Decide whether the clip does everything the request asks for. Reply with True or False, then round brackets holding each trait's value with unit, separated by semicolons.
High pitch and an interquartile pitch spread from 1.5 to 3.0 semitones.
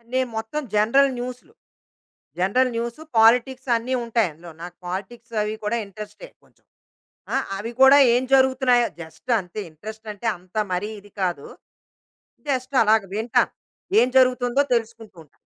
False (230 Hz; 3.7 semitones)